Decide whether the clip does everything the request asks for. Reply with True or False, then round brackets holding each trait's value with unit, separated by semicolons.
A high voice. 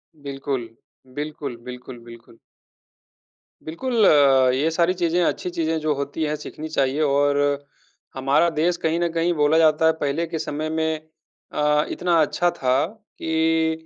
False (155 Hz)